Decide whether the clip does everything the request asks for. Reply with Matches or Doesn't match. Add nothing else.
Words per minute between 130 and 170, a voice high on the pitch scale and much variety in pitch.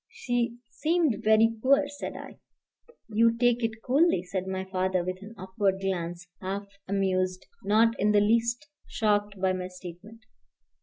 Doesn't match